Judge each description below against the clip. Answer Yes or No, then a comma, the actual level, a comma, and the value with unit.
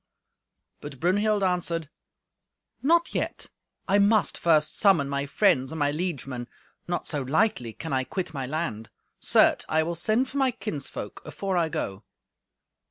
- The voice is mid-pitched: Yes, medium, 165 Hz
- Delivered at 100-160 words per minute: Yes, average, 150 wpm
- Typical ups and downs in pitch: No, wide, 6.1 semitones